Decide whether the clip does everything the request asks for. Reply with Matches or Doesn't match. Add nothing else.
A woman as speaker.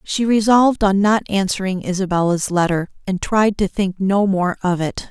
Matches